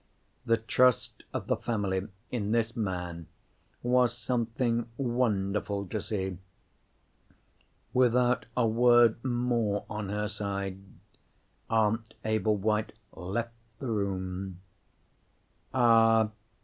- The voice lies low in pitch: Yes, low, 110 Hz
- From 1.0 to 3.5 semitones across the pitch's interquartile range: Yes, average, 3.0 semitones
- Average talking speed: No, slow, 95 wpm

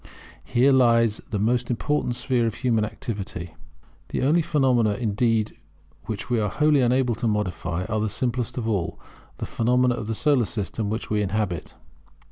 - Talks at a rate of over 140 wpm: Yes, average, 165 wpm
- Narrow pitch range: No, average, 3.0 semitones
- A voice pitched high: No, low, 115 Hz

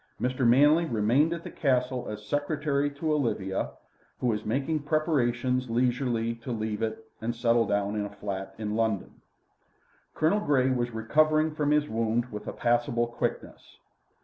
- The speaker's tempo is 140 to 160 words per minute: Yes, average, 155 wpm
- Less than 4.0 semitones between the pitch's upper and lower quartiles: No, average, 4.4 semitones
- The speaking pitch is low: Yes, low, 120 Hz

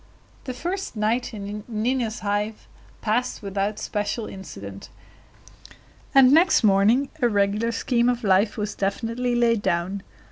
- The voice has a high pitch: Yes, high, 215 Hz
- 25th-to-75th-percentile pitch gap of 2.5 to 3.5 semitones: Yes, average, 3.2 semitones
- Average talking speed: No, slow, 130 wpm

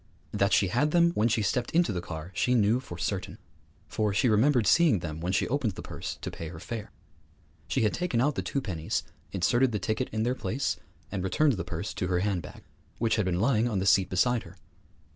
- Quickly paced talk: Yes, fast, 225 wpm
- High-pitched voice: No, low, 105 Hz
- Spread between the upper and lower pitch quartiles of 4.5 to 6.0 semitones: Yes, average, 5.1 semitones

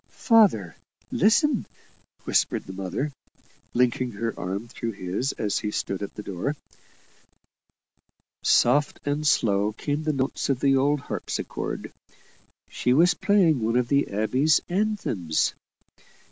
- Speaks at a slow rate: Yes, slow, 125 wpm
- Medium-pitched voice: No, low, 125 Hz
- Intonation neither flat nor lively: No, wide, 6.2 semitones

